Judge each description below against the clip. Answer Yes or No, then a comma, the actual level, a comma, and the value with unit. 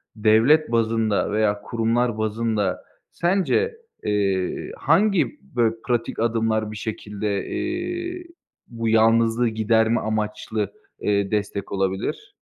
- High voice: No, low, 110 Hz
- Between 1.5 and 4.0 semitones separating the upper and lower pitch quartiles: Yes, narrow, 2.4 semitones